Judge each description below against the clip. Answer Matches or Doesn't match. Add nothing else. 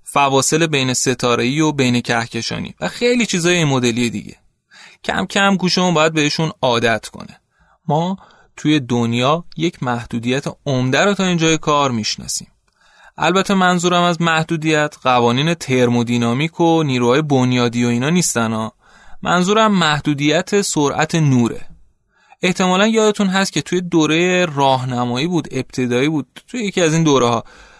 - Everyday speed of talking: Matches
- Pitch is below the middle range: Doesn't match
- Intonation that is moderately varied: Doesn't match